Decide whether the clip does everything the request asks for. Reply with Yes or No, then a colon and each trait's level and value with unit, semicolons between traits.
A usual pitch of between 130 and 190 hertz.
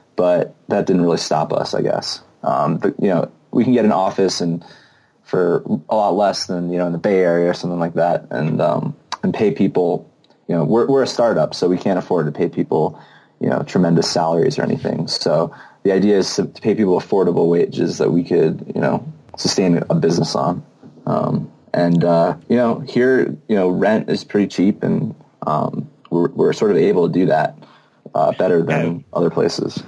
No: very low, 90 Hz